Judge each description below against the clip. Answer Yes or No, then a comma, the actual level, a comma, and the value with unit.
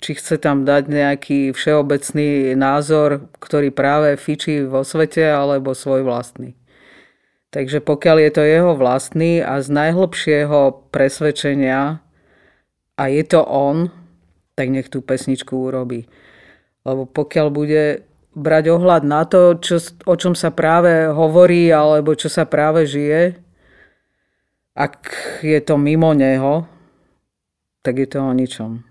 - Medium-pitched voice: Yes, medium, 150 Hz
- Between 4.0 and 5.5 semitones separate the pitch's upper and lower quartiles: No, average, 2.9 semitones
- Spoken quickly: No, average, 130 wpm